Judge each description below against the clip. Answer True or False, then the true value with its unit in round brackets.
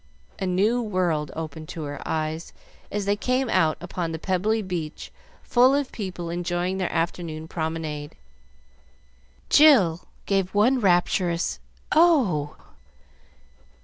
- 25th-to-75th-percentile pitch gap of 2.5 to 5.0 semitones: True (4.4 semitones)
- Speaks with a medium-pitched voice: True (180 Hz)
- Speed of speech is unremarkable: False (115 wpm)